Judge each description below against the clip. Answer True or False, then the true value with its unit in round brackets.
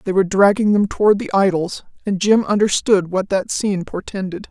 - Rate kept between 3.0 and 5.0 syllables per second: False (5.5 syllables/s)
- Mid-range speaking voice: False (195 Hz)